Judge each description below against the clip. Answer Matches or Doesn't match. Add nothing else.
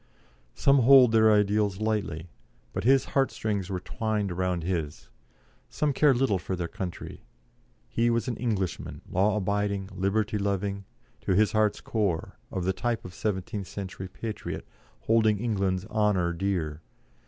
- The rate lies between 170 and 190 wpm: Doesn't match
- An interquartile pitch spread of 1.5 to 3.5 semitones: Matches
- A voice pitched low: Matches